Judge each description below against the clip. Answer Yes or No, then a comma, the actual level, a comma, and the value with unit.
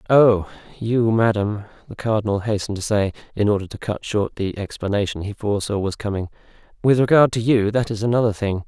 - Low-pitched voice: Yes, low, 105 Hz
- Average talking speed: Yes, average, 185 wpm